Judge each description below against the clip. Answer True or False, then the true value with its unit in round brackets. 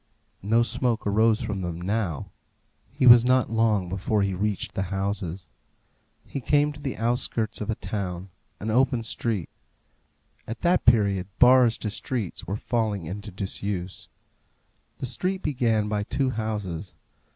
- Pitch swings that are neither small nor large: True (3.7 semitones)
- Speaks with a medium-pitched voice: False (110 Hz)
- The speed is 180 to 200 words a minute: False (145 wpm)